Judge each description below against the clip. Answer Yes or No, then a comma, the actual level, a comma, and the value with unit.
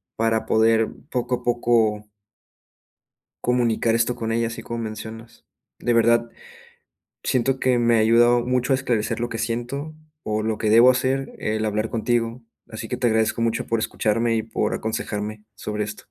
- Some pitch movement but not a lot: No, narrow, 1.6 semitones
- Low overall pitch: Yes, low, 115 Hz